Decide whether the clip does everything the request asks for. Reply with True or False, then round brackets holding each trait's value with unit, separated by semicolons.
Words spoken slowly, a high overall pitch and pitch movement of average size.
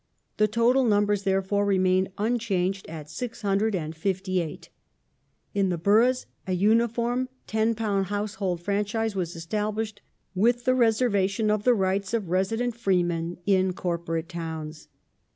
True (115 wpm; 200 Hz; 3.2 semitones)